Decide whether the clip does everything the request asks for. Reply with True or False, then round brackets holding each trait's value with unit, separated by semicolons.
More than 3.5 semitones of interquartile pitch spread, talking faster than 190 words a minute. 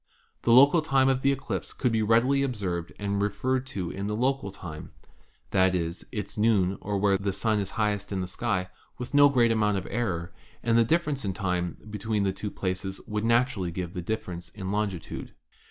True (4.1 semitones; 200 wpm)